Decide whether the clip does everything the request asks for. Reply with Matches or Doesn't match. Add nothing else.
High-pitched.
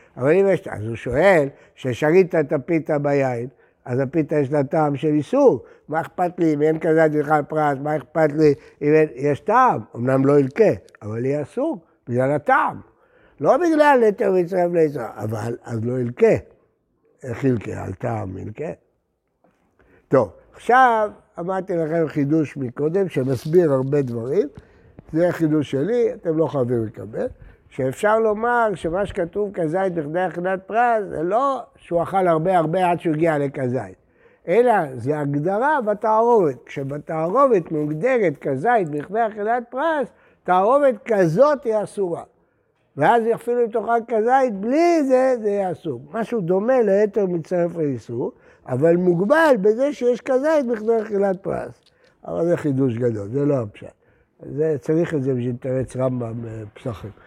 Doesn't match